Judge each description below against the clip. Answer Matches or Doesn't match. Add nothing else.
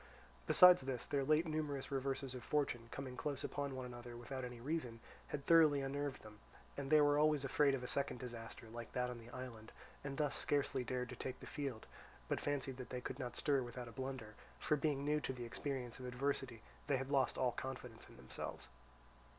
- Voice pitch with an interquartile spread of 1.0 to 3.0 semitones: Matches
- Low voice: Matches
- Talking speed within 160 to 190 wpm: Doesn't match